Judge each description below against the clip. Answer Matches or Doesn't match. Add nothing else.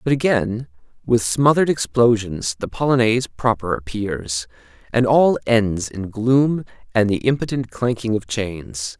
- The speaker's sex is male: Matches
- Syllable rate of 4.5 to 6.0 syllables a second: Doesn't match